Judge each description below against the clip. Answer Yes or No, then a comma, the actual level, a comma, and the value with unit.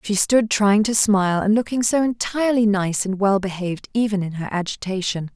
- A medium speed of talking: Yes, average, 190 wpm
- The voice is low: No, high, 205 Hz